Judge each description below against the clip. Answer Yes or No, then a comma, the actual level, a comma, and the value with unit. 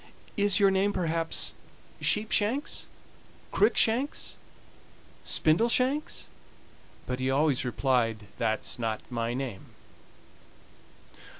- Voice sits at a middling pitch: Yes, medium, 160 Hz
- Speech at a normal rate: No, slow, 80 wpm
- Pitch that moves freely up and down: Yes, wide, 9.0 semitones